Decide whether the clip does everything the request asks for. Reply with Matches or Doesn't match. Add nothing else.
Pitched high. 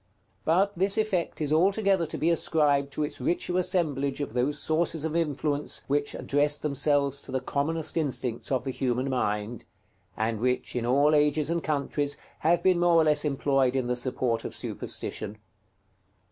Doesn't match